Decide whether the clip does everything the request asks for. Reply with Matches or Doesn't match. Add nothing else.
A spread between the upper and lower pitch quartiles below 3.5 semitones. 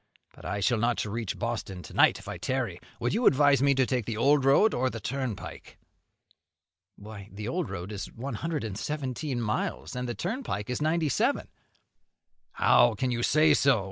Doesn't match